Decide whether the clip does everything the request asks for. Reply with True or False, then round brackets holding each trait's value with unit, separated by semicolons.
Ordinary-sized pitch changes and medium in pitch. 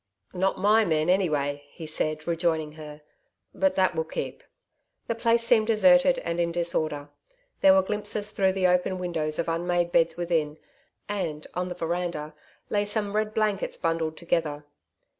True (4.3 semitones; 175 Hz)